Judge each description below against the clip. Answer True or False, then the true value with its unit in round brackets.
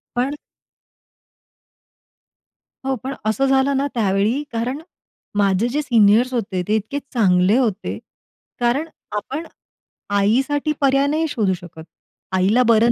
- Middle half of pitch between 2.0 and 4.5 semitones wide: False (5.0 semitones)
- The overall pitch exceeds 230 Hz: True (240 Hz)